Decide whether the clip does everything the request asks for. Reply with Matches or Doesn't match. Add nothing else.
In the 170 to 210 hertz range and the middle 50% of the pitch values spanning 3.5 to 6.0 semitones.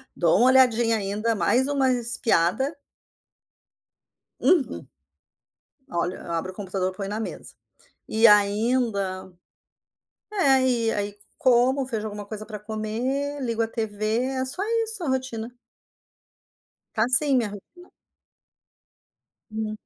Doesn't match